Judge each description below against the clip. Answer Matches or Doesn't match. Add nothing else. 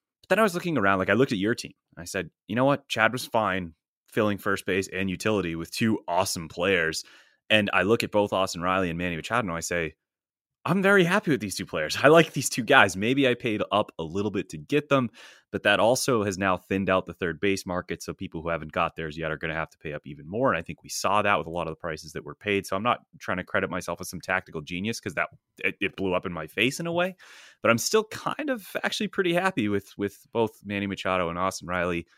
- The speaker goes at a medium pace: Doesn't match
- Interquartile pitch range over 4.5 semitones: Matches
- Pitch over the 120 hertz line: Doesn't match